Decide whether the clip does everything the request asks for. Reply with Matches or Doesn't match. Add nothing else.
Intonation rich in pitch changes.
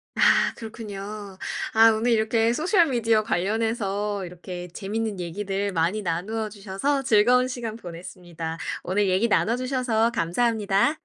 Doesn't match